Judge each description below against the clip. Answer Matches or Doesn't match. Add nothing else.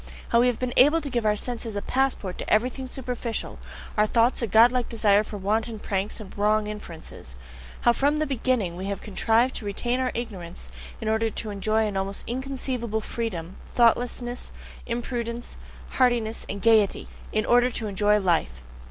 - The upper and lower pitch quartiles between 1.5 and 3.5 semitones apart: Matches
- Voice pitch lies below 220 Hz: Doesn't match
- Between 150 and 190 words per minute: Matches